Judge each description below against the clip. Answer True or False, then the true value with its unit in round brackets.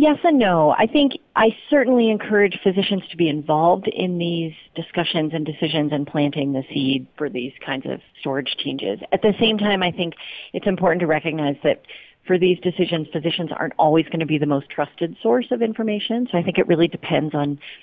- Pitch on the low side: False (170 Hz)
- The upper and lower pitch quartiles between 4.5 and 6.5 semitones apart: True (5.0 semitones)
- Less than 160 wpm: False (200 wpm)